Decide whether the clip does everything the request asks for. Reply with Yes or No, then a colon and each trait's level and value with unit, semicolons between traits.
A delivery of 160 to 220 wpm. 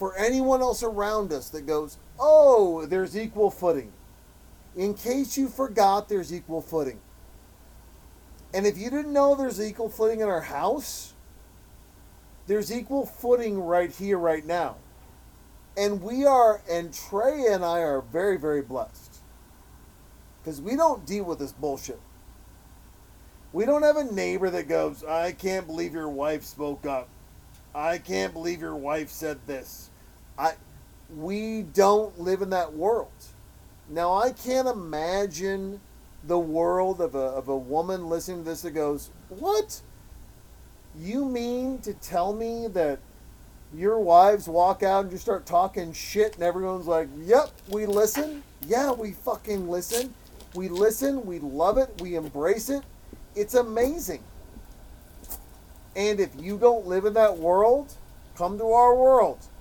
No: average, 145 wpm